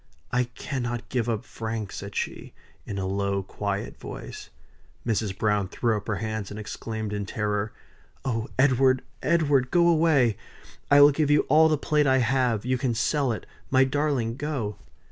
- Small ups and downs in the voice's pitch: No, average, 4.4 semitones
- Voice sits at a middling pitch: No, low, 120 Hz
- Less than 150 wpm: No, average, 170 wpm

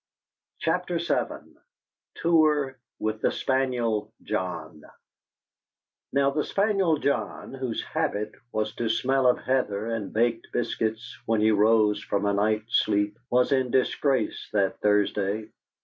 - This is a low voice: Yes, low, 115 Hz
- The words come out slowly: Yes, slow, 125 wpm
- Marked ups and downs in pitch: No, average, 4.0 semitones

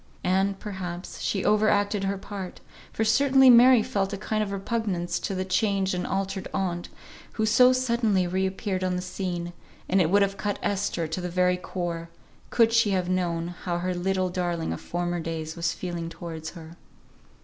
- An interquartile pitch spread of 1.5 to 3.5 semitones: Yes, narrow, 2.6 semitones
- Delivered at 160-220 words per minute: Yes, average, 180 wpm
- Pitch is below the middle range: No, medium, 185 Hz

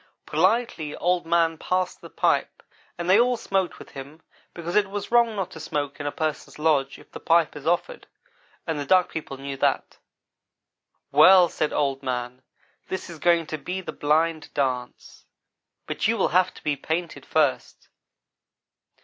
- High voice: No, medium, 165 Hz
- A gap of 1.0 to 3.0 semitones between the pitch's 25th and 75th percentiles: No, average, 4.0 semitones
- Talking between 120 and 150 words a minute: No, average, 170 wpm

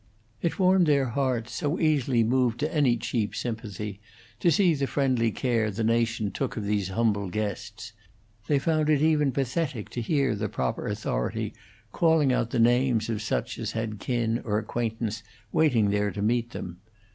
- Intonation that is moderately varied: Yes, average, 4.3 semitones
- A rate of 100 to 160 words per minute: No, average, 170 wpm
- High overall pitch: No, low, 115 Hz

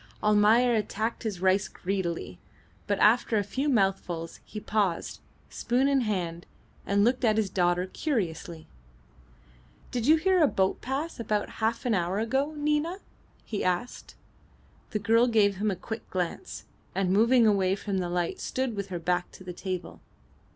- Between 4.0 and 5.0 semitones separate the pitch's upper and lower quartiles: Yes, average, 4.4 semitones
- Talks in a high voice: Yes, high, 210 Hz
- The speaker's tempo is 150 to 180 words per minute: Yes, average, 160 wpm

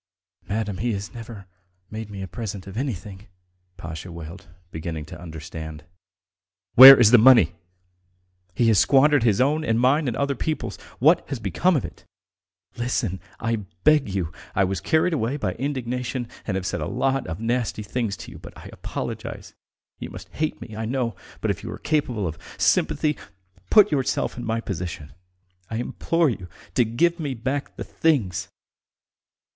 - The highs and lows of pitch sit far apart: Yes, wide, 5.7 semitones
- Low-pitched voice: Yes, low, 115 Hz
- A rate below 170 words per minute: No, average, 175 wpm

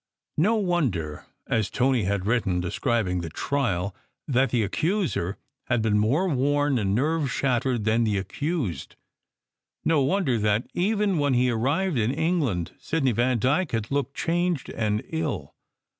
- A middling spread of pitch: No, wide, 6.5 semitones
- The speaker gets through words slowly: No, average, 145 wpm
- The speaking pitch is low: Yes, low, 125 Hz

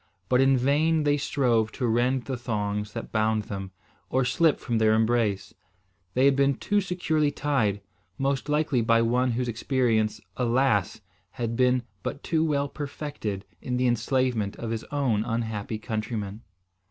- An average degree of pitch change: Yes, average, 3.9 semitones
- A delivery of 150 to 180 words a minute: Yes, average, 155 wpm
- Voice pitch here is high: No, low, 125 Hz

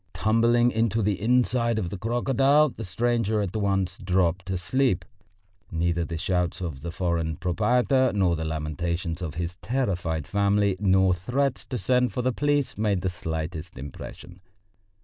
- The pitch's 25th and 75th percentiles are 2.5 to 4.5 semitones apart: No, wide, 5.5 semitones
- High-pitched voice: No, very low, 95 Hz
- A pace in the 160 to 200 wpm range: No, average, 150 wpm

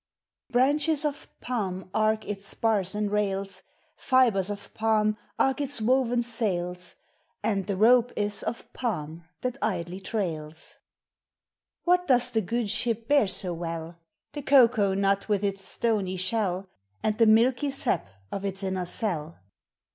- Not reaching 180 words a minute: Yes, average, 140 wpm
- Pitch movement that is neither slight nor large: Yes, average, 4.1 semitones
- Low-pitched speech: No, high, 210 Hz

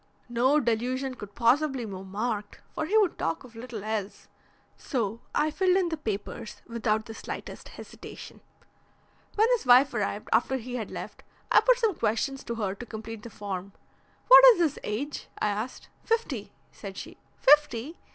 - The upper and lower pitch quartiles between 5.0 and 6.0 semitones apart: Yes, wide, 5.5 semitones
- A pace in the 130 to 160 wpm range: No, average, 170 wpm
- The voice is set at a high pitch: Yes, high, 235 Hz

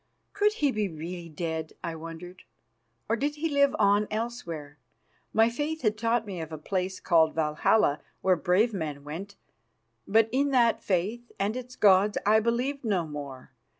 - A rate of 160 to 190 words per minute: Yes, average, 165 wpm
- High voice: Yes, high, 200 Hz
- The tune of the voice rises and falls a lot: Yes, wide, 6.1 semitones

